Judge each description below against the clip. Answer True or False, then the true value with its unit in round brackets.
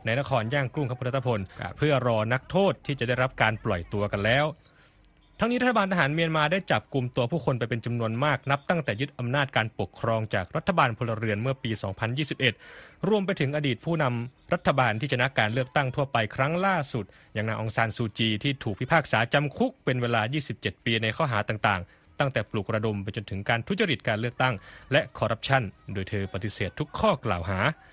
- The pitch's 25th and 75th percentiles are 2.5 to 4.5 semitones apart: False (5.1 semitones)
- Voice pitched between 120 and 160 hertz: True (125 Hz)